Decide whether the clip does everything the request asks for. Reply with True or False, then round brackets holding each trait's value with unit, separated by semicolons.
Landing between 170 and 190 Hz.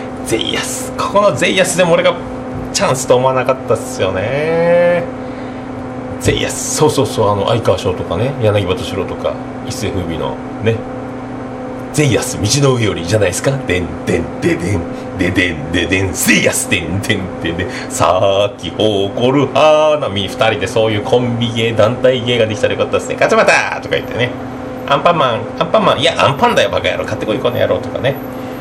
False (130 Hz)